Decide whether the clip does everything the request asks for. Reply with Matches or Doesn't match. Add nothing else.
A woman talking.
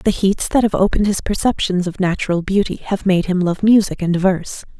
Matches